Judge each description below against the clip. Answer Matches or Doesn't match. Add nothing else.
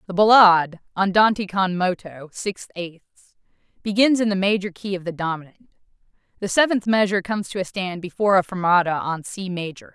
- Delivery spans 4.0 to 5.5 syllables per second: Doesn't match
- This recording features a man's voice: Doesn't match